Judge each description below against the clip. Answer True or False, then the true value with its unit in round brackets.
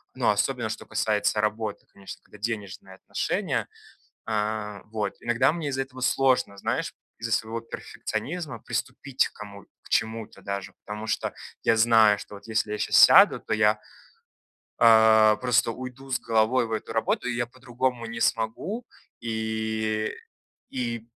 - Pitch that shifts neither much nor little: False (2.2 semitones)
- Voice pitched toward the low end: True (110 Hz)